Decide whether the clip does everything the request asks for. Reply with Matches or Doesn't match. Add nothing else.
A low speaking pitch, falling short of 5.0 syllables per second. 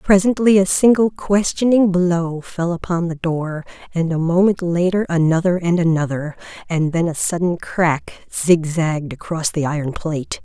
Doesn't match